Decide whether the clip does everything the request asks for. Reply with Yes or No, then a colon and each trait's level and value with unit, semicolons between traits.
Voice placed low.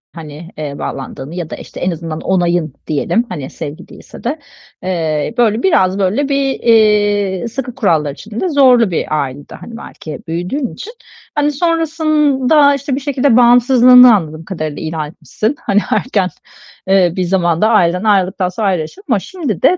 No: high, 205 Hz